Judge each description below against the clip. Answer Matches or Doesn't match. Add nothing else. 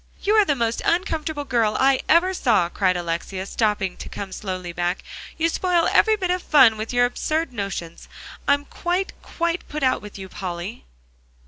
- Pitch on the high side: Matches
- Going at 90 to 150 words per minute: Doesn't match